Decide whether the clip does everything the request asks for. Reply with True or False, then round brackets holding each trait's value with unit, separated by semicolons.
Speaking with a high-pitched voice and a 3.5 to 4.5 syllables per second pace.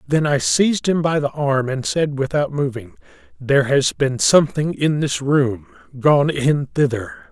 False (145 Hz; 4.4 syllables/s)